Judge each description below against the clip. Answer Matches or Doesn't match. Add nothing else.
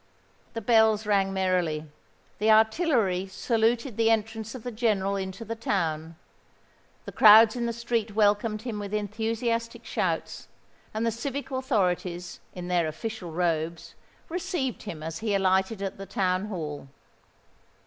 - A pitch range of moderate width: Matches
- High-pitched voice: Matches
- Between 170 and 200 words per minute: Doesn't match